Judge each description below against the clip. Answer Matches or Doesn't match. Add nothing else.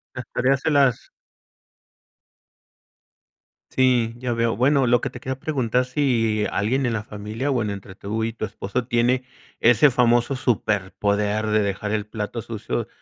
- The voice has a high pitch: Doesn't match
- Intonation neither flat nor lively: Matches